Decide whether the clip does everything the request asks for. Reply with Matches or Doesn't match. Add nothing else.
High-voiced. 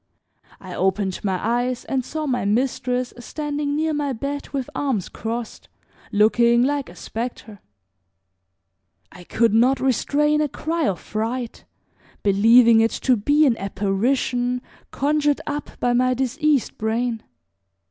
Matches